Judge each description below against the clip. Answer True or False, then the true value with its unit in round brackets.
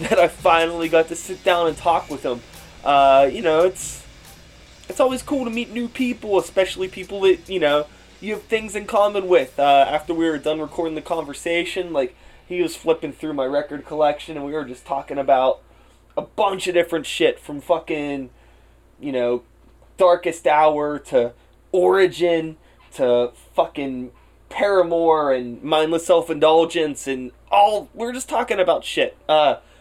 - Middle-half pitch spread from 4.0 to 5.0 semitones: True (4.6 semitones)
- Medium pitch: True (160 Hz)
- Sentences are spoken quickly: False (165 wpm)